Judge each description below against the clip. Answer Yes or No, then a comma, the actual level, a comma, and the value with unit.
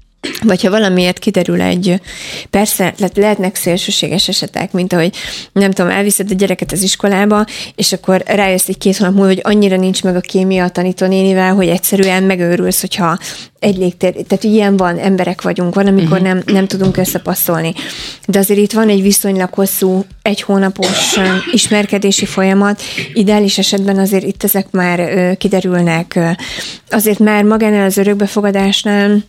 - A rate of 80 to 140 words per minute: No, average, 150 wpm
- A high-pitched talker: Yes, high, 195 Hz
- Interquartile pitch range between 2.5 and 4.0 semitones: No, narrow, 1.7 semitones